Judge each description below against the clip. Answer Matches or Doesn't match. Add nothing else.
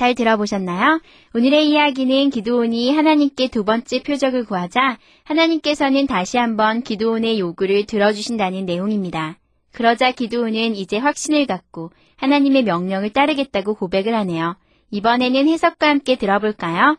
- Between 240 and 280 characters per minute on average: Doesn't match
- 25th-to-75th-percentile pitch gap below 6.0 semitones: Matches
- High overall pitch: Matches